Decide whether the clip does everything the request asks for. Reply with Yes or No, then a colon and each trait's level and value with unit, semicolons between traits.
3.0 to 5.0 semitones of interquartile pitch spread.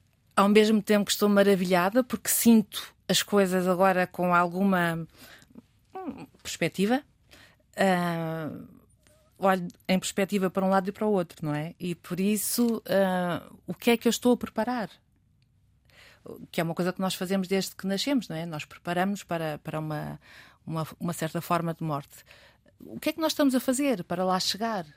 Yes: average, 4.1 semitones